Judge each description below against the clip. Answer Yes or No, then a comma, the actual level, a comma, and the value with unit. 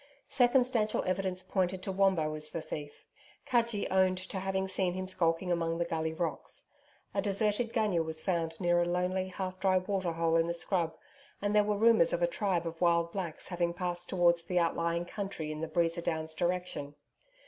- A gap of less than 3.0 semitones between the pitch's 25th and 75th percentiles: Yes, narrow, 2.4 semitones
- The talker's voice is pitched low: No, medium, 180 Hz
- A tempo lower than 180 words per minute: No, average, 185 wpm